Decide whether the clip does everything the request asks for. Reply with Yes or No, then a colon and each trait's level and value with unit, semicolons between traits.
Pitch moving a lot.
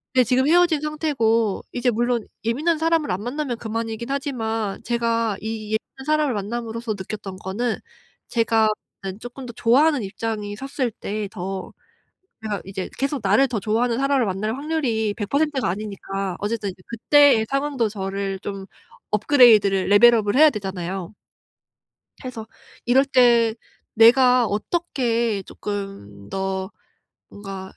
No: average, 4.2 semitones